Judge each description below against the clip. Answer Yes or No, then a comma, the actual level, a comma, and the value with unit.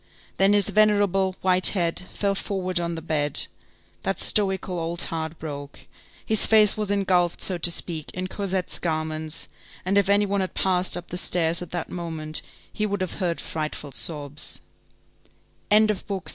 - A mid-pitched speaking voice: Yes, medium, 180 Hz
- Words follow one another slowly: No, average, 160 wpm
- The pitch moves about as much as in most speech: Yes, average, 3.2 semitones